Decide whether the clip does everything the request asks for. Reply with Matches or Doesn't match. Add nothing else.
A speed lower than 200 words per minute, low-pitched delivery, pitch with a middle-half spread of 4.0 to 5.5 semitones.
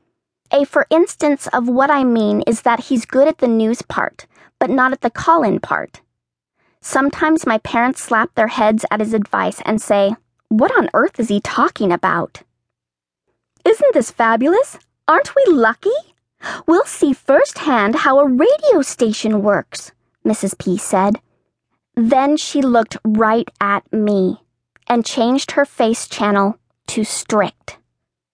Doesn't match